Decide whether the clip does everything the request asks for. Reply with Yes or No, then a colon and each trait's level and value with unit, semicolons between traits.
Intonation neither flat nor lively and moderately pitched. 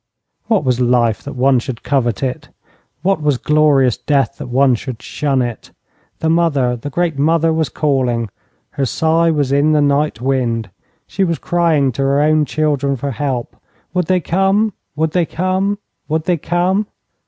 Yes: average, 4.1 semitones; medium, 145 Hz